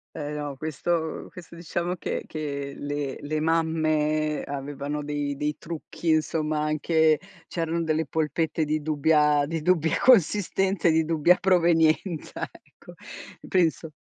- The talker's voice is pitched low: No, medium, 155 Hz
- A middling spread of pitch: No, narrow, 1.7 semitones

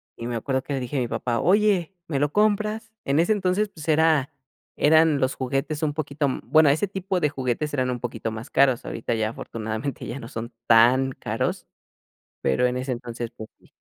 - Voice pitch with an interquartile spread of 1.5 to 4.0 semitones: No, average, 4.9 semitones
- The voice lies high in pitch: No, low, 135 Hz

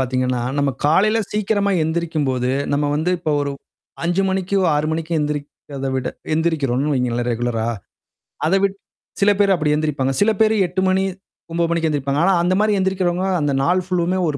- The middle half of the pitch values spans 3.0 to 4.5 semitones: No, average, 5.1 semitones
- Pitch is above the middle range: No, medium, 160 Hz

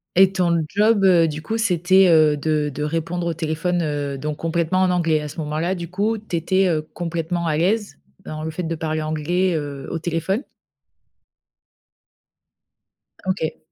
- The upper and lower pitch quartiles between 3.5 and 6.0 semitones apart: No, average, 2.9 semitones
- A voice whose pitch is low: No, medium, 165 Hz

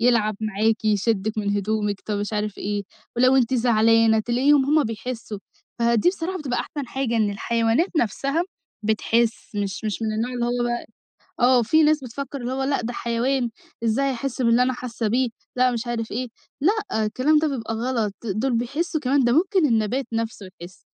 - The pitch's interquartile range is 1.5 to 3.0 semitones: No, average, 3.4 semitones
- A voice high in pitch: Yes, high, 235 Hz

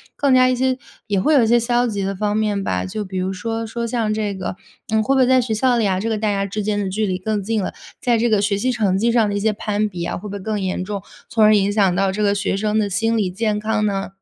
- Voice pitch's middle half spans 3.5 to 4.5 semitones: No, narrow, 2.4 semitones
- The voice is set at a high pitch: Yes, high, 210 Hz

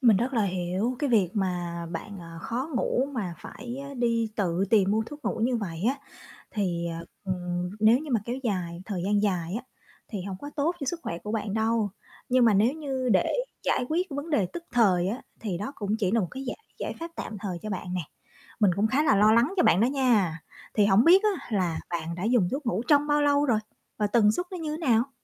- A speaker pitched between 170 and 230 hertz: Yes, high, 220 Hz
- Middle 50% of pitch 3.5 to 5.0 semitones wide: No, wide, 5.6 semitones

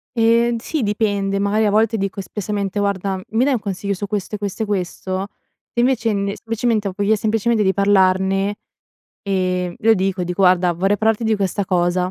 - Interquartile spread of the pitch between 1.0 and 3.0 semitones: Yes, narrow, 2.4 semitones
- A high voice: Yes, high, 200 Hz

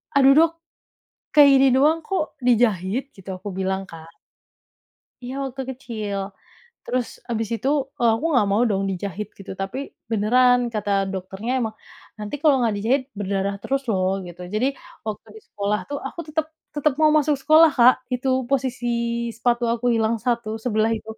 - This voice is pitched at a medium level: No, high, 235 Hz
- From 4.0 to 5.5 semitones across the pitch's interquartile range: Yes, average, 4.8 semitones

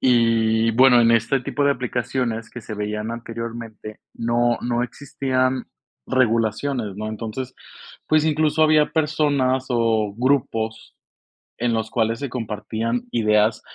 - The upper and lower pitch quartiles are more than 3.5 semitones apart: No, average, 2.7 semitones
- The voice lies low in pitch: Yes, low, 115 Hz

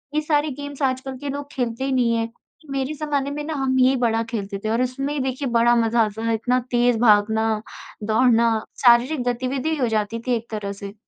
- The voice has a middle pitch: No, high, 245 Hz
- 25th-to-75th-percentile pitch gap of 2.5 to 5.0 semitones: Yes, average, 3.1 semitones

